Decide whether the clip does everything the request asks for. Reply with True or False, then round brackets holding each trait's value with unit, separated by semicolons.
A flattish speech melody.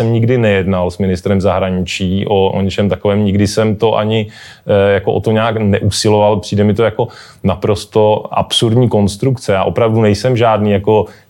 True (1.8 semitones)